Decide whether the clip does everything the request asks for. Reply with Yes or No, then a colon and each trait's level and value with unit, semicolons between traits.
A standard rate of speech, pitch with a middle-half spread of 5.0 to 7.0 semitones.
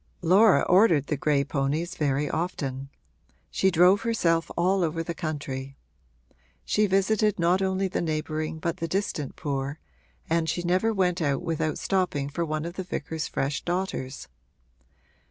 No: average, 150 wpm; average, 3.7 semitones